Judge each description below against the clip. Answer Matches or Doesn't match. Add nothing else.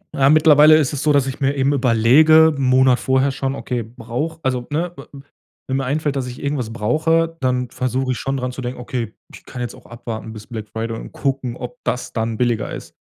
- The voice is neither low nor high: Doesn't match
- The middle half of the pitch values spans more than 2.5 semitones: Matches